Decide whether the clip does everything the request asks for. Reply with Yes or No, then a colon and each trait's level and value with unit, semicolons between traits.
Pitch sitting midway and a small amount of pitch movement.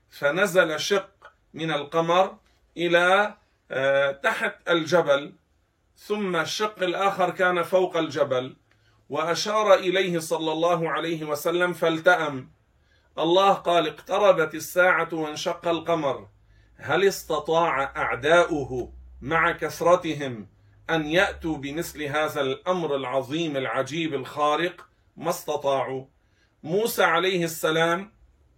No: medium, 165 Hz; average, 4.2 semitones